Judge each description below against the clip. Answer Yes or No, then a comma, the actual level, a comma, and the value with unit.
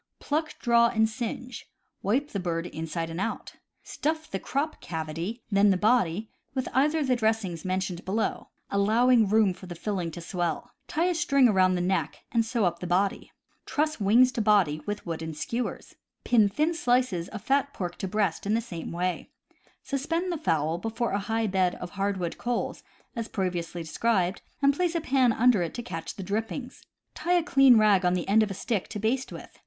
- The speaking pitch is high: Yes, high, 215 Hz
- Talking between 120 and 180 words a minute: No, average, 195 wpm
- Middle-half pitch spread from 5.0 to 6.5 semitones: Yes, wide, 5.6 semitones